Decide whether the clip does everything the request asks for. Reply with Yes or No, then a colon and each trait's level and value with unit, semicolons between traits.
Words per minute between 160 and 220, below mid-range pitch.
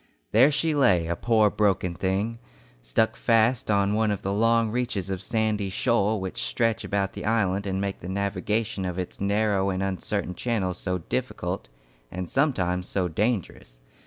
Yes: average, 165 wpm; low, 100 Hz